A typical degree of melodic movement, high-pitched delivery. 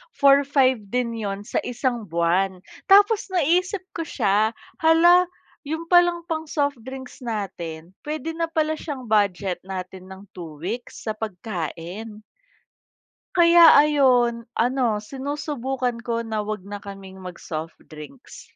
No: wide, 7.2 semitones; high, 235 Hz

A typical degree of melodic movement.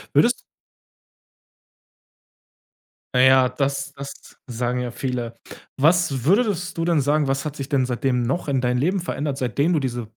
Yes: average, 3.3 semitones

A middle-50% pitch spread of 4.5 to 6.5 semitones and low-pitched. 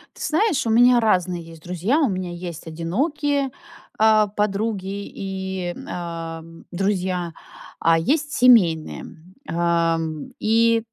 No: average, 5.1 semitones; high, 190 Hz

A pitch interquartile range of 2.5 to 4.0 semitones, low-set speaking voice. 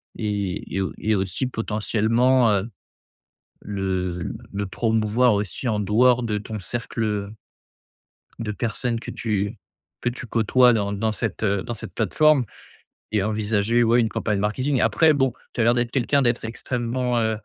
Yes: average, 2.8 semitones; low, 110 Hz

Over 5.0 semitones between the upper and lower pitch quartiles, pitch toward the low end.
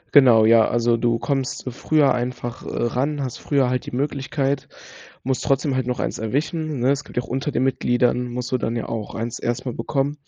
No: narrow, 2.4 semitones; low, 125 Hz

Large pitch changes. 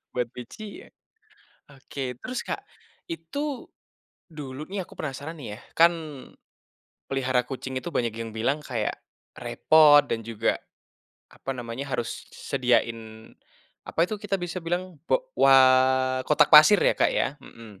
Yes: wide, 5.7 semitones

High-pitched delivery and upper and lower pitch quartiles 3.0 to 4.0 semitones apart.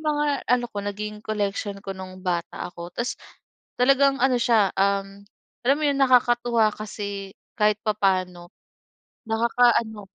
Yes: high, 215 Hz; average, 3.7 semitones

